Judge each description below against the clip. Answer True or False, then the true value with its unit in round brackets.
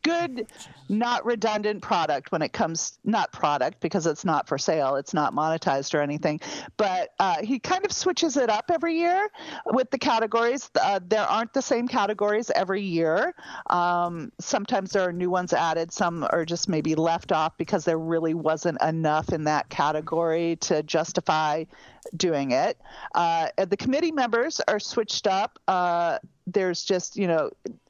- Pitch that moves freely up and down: True (6.3 semitones)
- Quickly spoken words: False (165 wpm)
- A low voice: False (185 Hz)